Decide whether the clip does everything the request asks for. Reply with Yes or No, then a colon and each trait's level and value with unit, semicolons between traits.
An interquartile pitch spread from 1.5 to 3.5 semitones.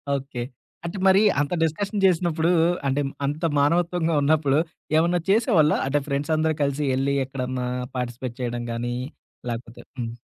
No: average, 4.6 semitones